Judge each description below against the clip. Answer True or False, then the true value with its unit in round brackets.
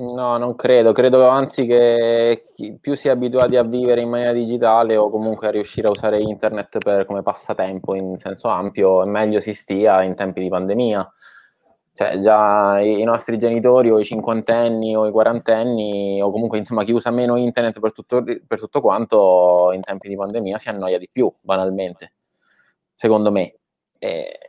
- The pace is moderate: False (175 wpm)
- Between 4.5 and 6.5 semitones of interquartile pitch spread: False (3.0 semitones)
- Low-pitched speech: True (110 Hz)